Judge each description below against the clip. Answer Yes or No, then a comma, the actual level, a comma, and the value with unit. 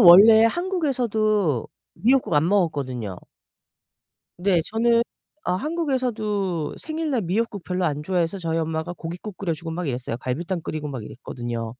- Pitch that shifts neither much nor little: No, wide, 6.2 semitones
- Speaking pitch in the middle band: Yes, medium, 180 Hz